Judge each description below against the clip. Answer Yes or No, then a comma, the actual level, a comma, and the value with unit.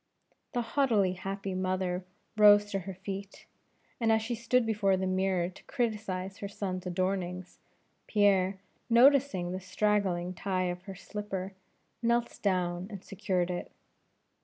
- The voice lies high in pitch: Yes, high, 195 Hz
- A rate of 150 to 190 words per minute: No, slow, 135 wpm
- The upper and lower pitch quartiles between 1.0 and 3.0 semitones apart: Yes, narrow, 2.4 semitones